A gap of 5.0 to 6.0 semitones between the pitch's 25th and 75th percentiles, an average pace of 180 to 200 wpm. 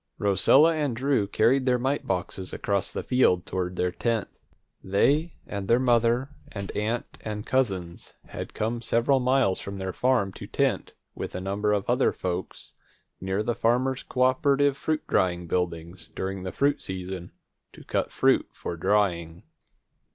No: wide, 5.5 semitones; average, 155 wpm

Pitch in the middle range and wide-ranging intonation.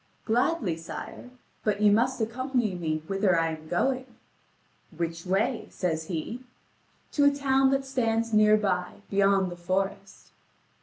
No: high, 205 Hz; wide, 5.9 semitones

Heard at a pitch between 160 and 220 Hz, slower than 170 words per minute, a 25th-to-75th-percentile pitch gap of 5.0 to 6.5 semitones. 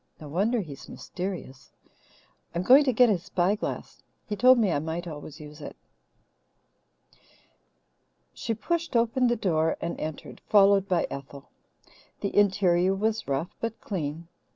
Yes: high, 190 Hz; average, 140 wpm; wide, 5.6 semitones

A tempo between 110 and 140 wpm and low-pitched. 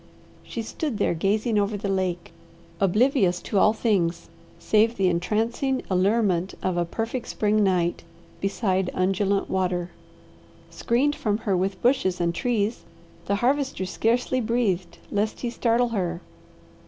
No: slow, 135 wpm; high, 205 Hz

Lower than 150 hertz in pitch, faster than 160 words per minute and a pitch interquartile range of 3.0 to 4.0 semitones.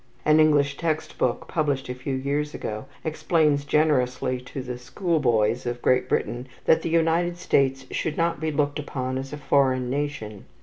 Yes: medium, 140 Hz; average, 175 wpm; average, 3.4 semitones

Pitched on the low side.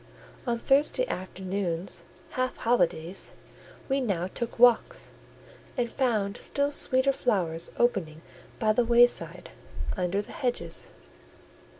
No: high, 230 Hz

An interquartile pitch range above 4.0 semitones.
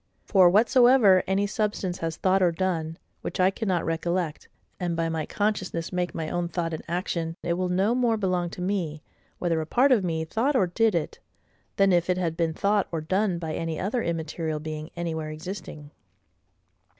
No: average, 3.0 semitones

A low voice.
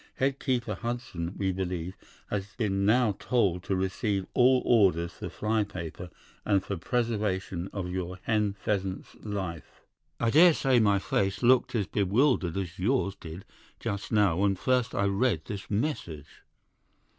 Yes: low, 100 Hz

